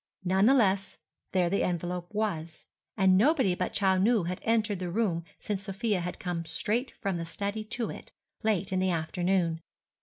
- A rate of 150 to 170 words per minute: No, average, 180 wpm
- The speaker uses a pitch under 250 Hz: Yes, high, 190 Hz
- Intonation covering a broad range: No, average, 3.2 semitones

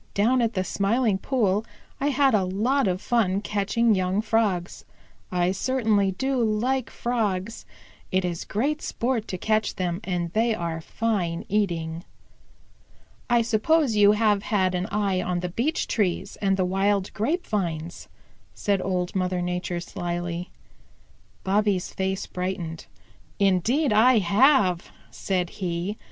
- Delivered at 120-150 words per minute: Yes, average, 140 wpm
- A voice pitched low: No, high, 200 Hz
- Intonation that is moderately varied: Yes, average, 3.7 semitones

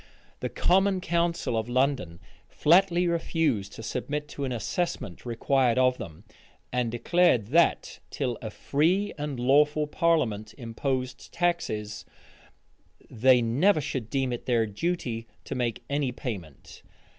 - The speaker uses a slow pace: Yes, slow, 130 wpm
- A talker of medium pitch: No, low, 130 Hz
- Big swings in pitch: Yes, wide, 6.1 semitones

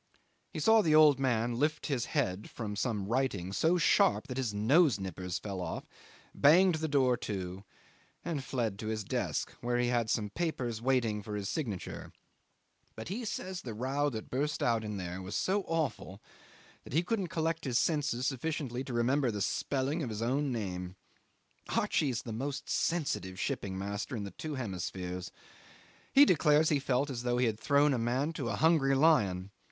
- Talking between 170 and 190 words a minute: Yes, average, 180 wpm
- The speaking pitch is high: No, low, 125 Hz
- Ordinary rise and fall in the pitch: No, wide, 5.9 semitones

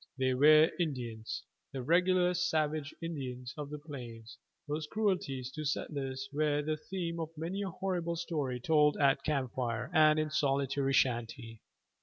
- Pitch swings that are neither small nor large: Yes, average, 3.7 semitones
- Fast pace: No, average, 150 wpm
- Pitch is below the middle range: No, medium, 150 Hz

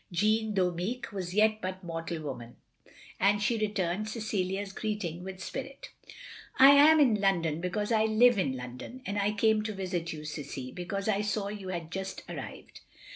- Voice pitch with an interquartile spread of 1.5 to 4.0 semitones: Yes, average, 3.6 semitones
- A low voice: No, high, 195 Hz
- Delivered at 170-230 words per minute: Yes, average, 175 wpm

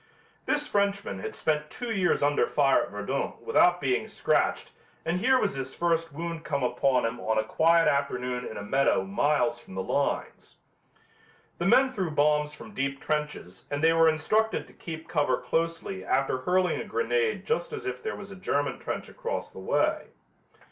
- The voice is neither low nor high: Yes, medium, 155 Hz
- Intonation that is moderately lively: No, wide, 6.0 semitones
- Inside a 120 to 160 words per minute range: No, average, 180 wpm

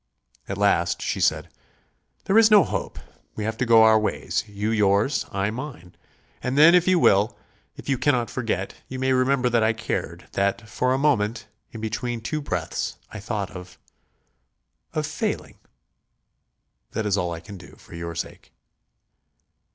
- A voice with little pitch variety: No, average, 4.4 semitones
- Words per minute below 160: No, average, 165 wpm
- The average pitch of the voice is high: No, low, 110 Hz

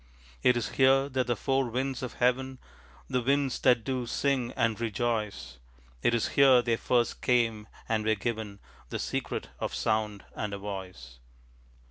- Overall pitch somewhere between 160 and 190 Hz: No, low, 120 Hz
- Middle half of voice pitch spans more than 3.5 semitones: No, average, 3.2 semitones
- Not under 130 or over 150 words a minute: No, average, 160 wpm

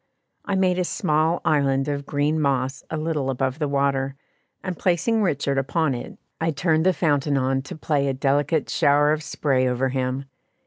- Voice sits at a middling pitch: Yes, medium, 145 Hz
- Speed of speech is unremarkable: Yes, average, 180 wpm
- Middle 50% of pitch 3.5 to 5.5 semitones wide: No, average, 2.9 semitones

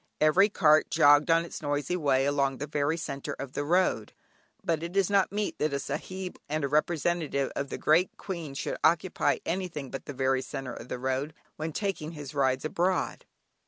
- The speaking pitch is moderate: Yes, medium, 150 Hz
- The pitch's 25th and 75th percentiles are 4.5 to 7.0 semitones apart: No, average, 3.7 semitones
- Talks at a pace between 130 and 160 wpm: No, average, 195 wpm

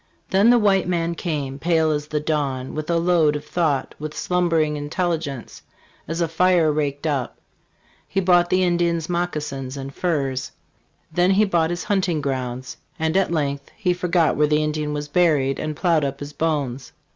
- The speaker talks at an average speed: Yes, average, 180 wpm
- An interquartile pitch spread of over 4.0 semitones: No, average, 3.2 semitones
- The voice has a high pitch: No, medium, 155 Hz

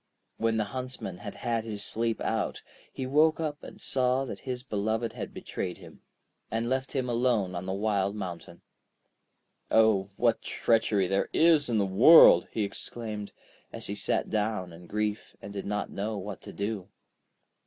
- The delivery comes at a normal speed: Yes, average, 170 wpm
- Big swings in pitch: No, average, 3.6 semitones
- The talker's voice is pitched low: Yes, low, 110 Hz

